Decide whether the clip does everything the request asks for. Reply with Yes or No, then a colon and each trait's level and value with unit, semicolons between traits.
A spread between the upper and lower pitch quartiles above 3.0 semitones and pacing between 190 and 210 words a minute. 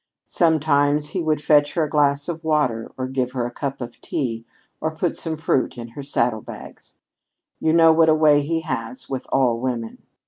Yes: average, 3.8 semitones; average, 200 wpm